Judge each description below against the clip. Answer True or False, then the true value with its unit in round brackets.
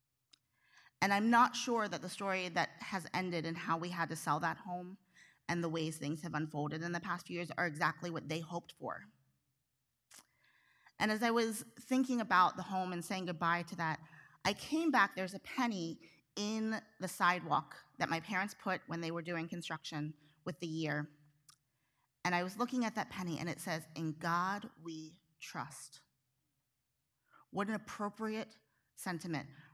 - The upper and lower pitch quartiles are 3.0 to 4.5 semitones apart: True (3.8 semitones)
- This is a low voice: False (170 Hz)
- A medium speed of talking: True (175 wpm)